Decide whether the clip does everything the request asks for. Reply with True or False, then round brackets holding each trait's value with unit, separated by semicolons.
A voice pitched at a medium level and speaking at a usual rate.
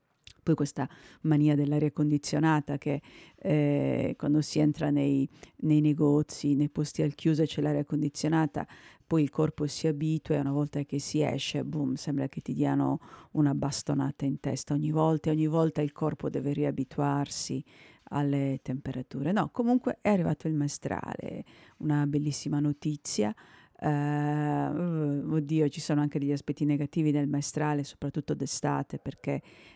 True (145 Hz; 145 wpm)